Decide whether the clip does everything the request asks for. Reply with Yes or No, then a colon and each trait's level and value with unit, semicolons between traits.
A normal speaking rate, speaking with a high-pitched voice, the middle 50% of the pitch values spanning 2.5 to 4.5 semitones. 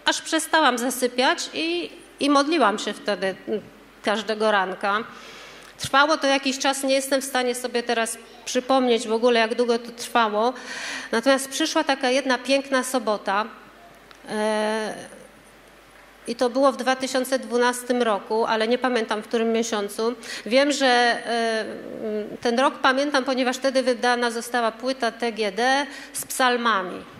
Yes: average, 130 wpm; high, 245 Hz; average, 3.0 semitones